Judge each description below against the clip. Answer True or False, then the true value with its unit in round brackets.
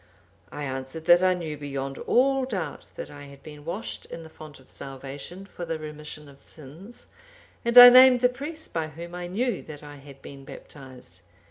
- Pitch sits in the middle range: True (155 Hz)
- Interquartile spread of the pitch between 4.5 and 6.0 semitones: True (5.6 semitones)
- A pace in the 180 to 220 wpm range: True (195 wpm)